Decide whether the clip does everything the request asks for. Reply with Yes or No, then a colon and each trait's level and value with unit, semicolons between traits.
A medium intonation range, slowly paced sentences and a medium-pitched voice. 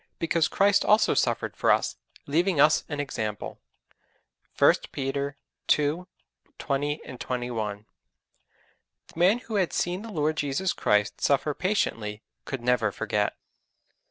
No: wide, 6.3 semitones; slow, 125 wpm; medium, 145 Hz